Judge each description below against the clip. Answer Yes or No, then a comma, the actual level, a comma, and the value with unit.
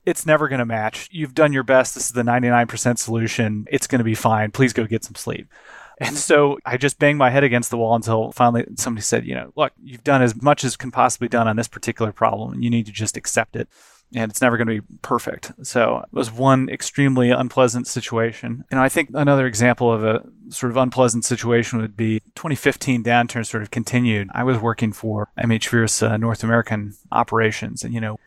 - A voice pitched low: Yes, low, 120 Hz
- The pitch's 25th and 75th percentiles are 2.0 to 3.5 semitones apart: Yes, narrow, 2.4 semitones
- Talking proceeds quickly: Yes, fast, 220 wpm